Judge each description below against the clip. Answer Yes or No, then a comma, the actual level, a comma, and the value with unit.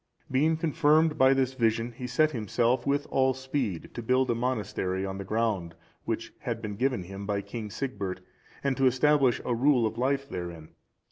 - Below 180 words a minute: No, average, 190 wpm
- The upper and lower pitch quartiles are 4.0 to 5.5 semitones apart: Yes, average, 4.4 semitones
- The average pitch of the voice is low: Yes, low, 125 Hz